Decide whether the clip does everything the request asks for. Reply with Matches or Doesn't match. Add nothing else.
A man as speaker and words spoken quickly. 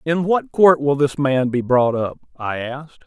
Matches